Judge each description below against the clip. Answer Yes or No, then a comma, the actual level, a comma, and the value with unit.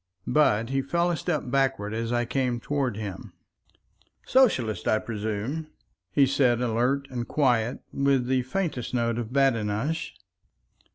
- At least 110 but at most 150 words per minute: Yes, average, 145 wpm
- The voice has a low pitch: Yes, low, 125 Hz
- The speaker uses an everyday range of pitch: Yes, average, 3.4 semitones